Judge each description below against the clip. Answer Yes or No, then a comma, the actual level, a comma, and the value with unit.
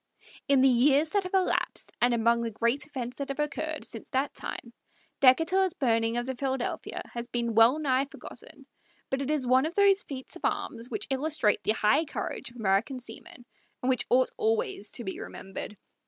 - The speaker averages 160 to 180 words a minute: No, average, 190 wpm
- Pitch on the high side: Yes, very high, 255 Hz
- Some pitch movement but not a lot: Yes, average, 3.9 semitones